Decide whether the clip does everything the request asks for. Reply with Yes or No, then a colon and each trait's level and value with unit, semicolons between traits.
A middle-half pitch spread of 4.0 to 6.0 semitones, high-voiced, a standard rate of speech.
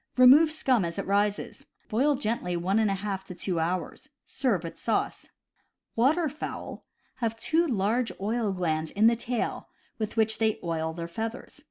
Yes: average, 5.2 semitones; high, 220 Hz; average, 165 wpm